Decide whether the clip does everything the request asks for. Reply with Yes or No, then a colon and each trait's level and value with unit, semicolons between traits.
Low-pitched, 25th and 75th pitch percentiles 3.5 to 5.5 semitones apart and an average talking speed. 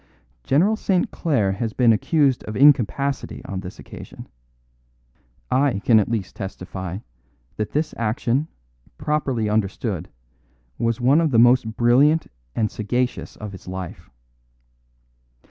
No: low, 115 Hz; average, 4.9 semitones; slow, 125 wpm